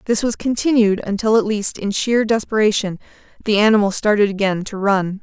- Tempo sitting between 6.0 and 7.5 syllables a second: No, 5.5 syllables/s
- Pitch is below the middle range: No, high, 210 Hz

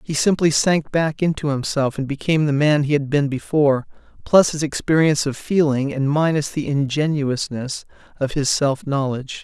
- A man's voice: Yes, male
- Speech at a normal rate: Yes, average, 170 wpm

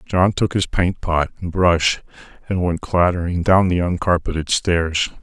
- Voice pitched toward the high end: No, very low, 85 Hz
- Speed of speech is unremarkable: Yes, average, 160 wpm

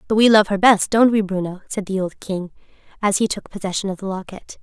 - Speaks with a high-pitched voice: Yes, high, 200 Hz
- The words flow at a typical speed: No, fast, 245 wpm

